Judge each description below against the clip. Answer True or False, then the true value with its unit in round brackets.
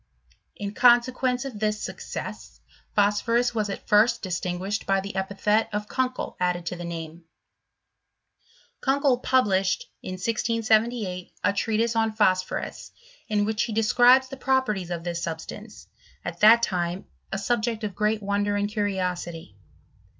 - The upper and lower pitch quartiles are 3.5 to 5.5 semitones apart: True (3.8 semitones)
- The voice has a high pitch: True (210 Hz)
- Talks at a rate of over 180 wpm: False (135 wpm)